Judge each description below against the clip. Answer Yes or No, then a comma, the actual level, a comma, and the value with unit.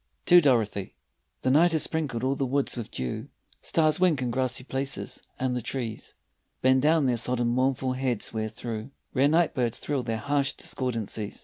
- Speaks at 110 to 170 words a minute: No, average, 180 wpm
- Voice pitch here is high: No, low, 130 Hz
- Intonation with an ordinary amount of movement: Yes, average, 3.1 semitones